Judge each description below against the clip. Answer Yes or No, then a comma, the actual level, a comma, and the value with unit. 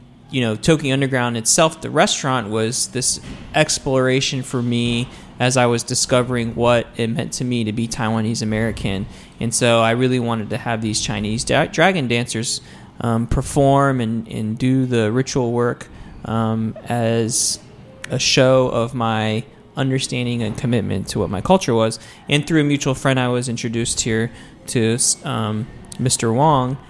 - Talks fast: No, average, 160 wpm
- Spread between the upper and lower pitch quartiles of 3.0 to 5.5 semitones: No, narrow, 2.5 semitones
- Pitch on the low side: Yes, low, 120 Hz